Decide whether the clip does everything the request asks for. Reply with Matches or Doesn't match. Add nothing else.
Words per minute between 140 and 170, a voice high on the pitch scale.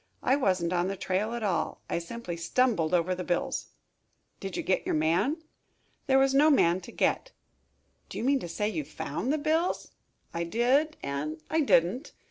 Doesn't match